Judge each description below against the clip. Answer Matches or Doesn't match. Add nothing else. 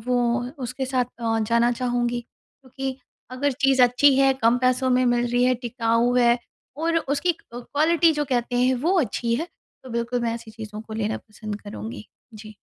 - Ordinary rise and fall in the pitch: Doesn't match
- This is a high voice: Matches